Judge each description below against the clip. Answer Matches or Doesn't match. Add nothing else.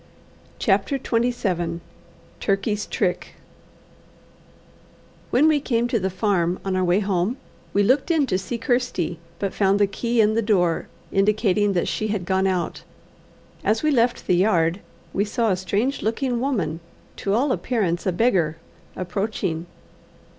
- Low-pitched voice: Doesn't match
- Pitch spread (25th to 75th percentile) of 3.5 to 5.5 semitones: Matches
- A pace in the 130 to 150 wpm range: Matches